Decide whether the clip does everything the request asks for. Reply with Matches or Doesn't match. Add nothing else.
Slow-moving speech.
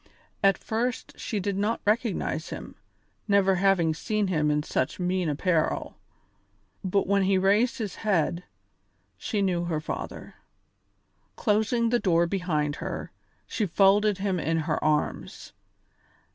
Matches